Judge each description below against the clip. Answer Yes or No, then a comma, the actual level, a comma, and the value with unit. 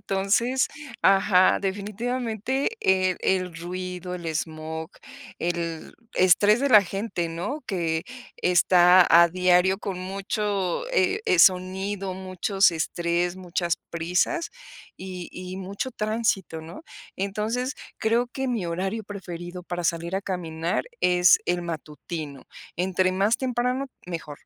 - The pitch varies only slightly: No, average, 3.0 semitones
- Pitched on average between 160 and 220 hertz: Yes, medium, 185 Hz